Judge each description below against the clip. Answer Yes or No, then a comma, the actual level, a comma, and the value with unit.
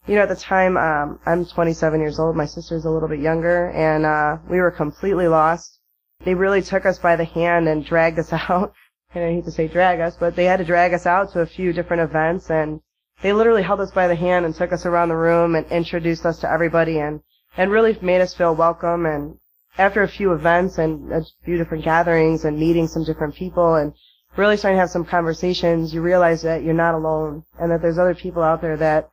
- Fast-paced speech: Yes, fast, 235 wpm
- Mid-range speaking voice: Yes, medium, 170 Hz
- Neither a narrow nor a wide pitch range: No, narrow, 1.8 semitones